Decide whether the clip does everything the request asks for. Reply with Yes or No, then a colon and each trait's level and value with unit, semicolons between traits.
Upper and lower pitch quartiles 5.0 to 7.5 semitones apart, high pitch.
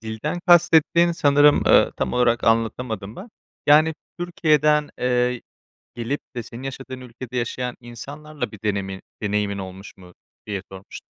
No: average, 5.3 semitones; low, 125 Hz